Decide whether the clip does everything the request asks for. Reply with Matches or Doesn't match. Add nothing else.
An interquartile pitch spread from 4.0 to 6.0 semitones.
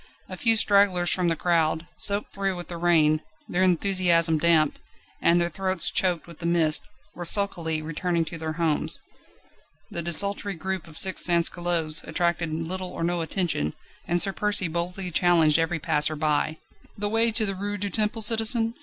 Doesn't match